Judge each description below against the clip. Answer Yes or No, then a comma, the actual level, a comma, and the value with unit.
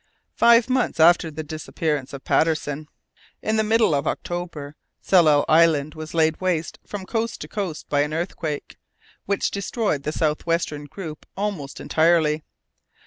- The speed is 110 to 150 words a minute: Yes, average, 145 wpm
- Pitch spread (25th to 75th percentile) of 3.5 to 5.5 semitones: Yes, average, 3.9 semitones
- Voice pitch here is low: No, medium, 160 Hz